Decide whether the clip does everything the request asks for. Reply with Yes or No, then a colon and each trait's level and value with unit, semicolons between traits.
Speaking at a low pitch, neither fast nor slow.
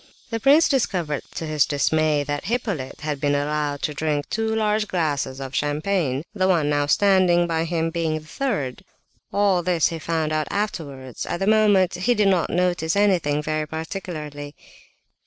No: medium, 160 Hz; average, 170 wpm